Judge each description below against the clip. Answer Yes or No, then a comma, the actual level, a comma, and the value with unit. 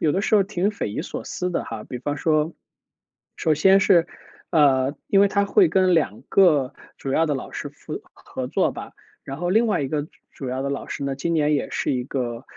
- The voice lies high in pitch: No, medium, 150 Hz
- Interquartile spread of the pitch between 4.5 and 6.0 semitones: Yes, wide, 5.5 semitones